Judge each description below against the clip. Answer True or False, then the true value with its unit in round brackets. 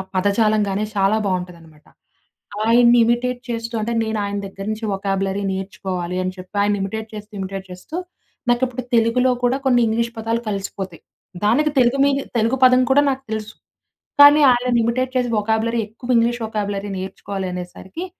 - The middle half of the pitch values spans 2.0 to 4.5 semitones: True (3.7 semitones)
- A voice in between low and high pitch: False (220 Hz)